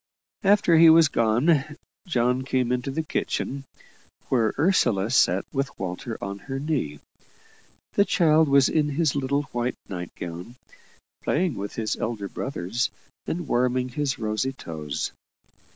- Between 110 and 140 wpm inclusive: Yes, slow, 135 wpm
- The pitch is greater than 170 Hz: No, low, 130 Hz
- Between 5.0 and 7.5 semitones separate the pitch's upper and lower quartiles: Yes, average, 5.3 semitones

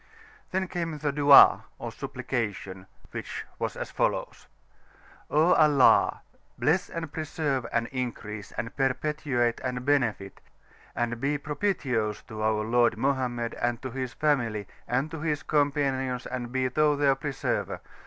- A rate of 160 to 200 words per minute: No, slow, 135 wpm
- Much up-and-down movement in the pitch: No, average, 3.7 semitones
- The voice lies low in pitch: Yes, low, 130 Hz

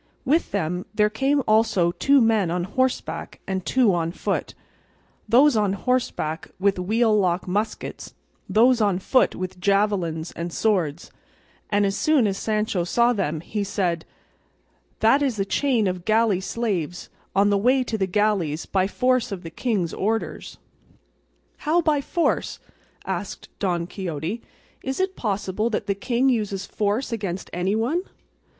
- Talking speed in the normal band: Yes, average, 150 wpm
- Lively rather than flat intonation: No, average, 4.4 semitones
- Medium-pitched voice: No, high, 205 Hz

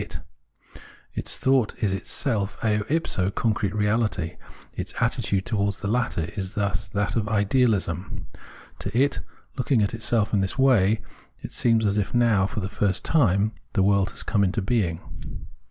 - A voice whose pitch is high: No, low, 105 Hz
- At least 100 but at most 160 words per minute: Yes, average, 155 wpm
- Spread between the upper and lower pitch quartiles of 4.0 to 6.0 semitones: No, average, 2.8 semitones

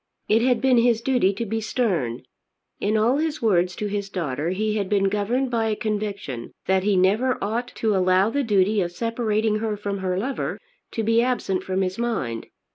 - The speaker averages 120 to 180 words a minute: No, average, 200 wpm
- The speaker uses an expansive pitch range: No, average, 3.4 semitones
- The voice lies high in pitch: Yes, high, 210 Hz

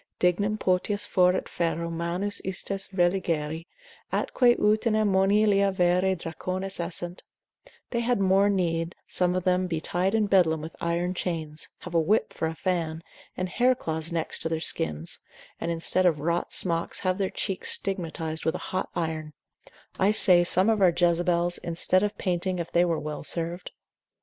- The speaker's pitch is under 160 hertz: No, medium, 180 Hz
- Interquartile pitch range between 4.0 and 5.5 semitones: No, narrow, 2.6 semitones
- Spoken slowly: No, average, 165 wpm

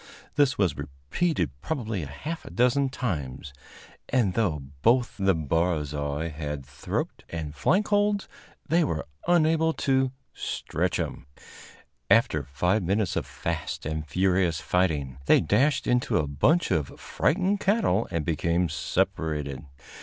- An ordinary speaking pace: No, slow, 130 wpm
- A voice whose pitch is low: Yes, very low, 90 Hz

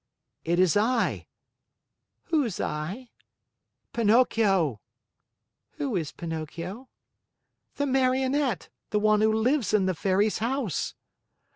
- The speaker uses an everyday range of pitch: No, wide, 5.7 semitones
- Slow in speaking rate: Yes, slow, 100 wpm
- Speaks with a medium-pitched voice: No, high, 215 Hz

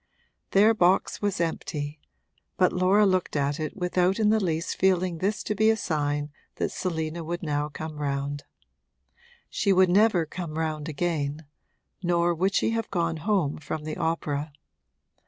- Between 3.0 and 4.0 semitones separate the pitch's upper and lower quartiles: Yes, average, 3.6 semitones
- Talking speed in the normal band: Yes, average, 155 wpm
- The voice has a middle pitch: Yes, medium, 170 Hz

